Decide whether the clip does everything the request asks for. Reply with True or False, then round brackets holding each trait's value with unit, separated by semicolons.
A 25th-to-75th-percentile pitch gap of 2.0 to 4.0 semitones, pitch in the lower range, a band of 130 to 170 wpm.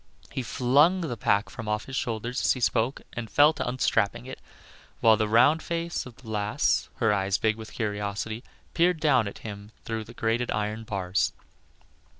False (3.6 semitones; 115 Hz; 180 wpm)